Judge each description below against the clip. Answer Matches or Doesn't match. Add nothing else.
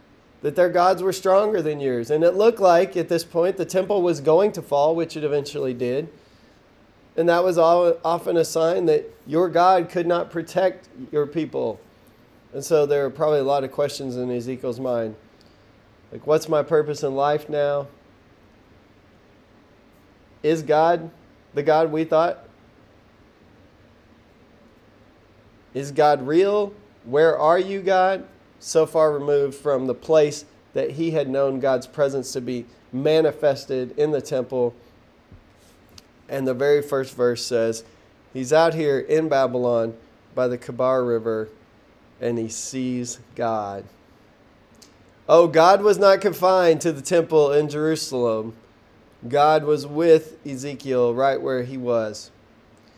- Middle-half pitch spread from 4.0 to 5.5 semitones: Matches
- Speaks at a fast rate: Doesn't match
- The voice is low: Doesn't match